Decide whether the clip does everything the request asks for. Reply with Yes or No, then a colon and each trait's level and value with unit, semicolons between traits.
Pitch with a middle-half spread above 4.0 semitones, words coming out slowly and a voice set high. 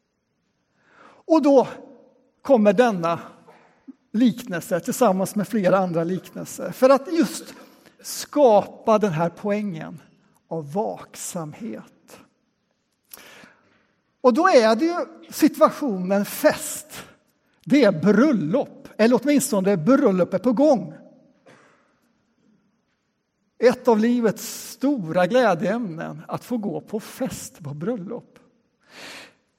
Yes: average, 4.7 semitones; slow, 95 wpm; high, 235 Hz